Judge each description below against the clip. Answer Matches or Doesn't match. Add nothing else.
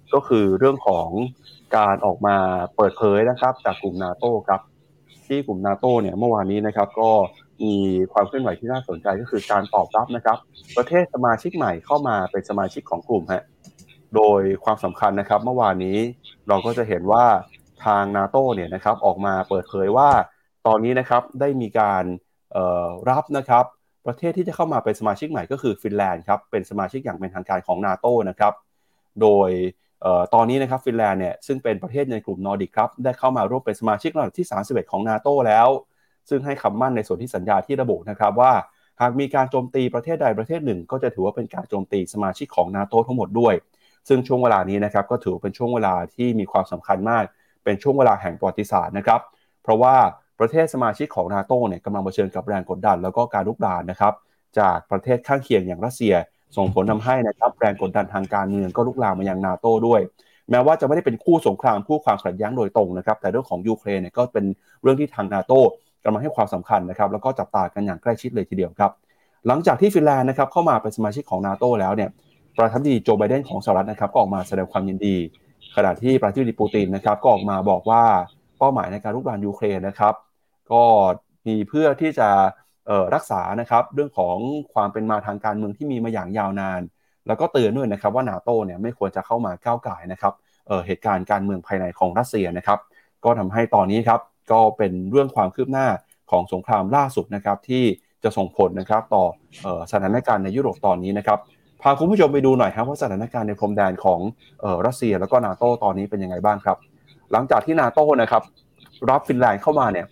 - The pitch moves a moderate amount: Matches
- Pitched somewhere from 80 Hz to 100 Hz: Doesn't match